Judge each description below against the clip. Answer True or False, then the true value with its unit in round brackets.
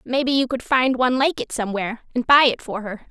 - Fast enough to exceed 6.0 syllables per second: True (6.4 syllables/s)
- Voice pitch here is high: True (245 Hz)